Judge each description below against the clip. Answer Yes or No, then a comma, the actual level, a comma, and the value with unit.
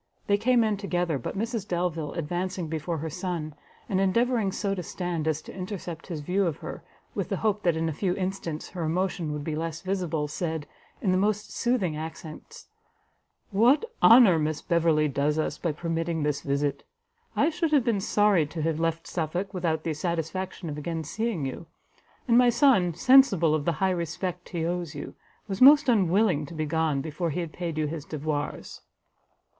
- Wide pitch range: No, average, 3.8 semitones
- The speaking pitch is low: No, medium, 170 Hz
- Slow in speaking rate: No, average, 190 wpm